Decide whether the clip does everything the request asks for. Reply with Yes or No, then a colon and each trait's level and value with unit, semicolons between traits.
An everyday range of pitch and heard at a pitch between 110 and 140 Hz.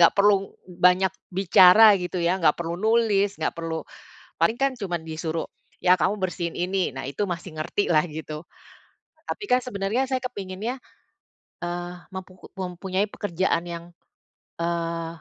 No: average, 3.0 semitones; medium, 185 Hz